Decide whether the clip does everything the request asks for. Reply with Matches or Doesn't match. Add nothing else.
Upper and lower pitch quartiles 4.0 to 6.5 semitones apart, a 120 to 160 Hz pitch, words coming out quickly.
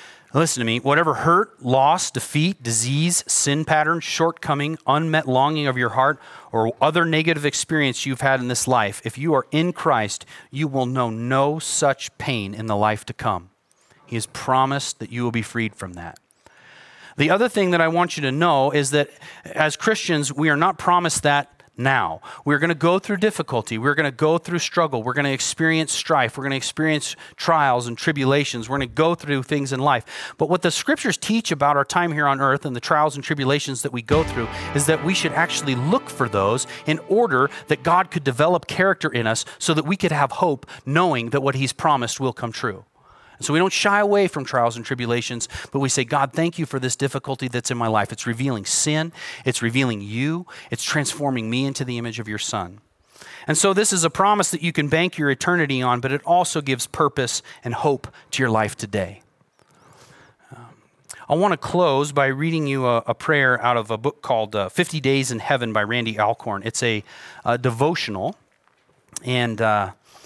Matches